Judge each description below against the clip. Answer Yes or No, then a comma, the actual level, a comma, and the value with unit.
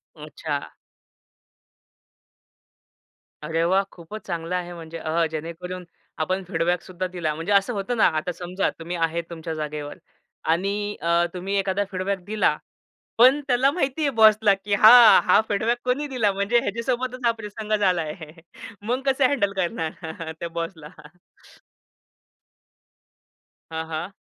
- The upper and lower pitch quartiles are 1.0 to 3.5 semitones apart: No, average, 4.6 semitones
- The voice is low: No, medium, 185 Hz